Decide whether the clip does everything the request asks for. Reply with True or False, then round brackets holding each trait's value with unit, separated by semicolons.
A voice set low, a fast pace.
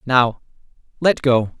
False (130 Hz; 115 wpm)